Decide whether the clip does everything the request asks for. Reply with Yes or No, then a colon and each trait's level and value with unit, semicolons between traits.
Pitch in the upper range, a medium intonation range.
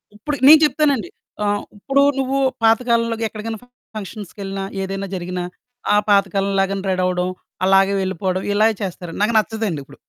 Yes: high, 200 Hz; average, 3.0 semitones